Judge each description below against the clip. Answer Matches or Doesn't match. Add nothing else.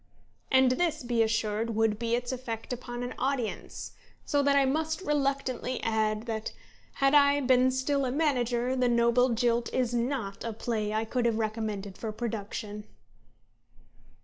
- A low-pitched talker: Doesn't match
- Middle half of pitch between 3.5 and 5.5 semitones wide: Doesn't match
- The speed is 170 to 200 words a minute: Doesn't match